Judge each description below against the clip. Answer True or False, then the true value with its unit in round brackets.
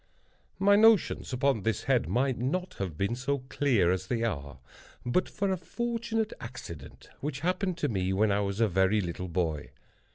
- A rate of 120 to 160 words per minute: False (175 wpm)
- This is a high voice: False (120 Hz)